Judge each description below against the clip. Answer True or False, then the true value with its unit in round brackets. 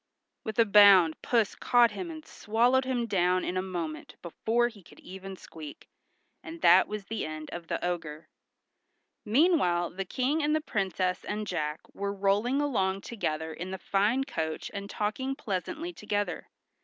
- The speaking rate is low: False (165 wpm)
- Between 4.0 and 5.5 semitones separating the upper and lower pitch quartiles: True (5.1 semitones)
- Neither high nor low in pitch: False (200 Hz)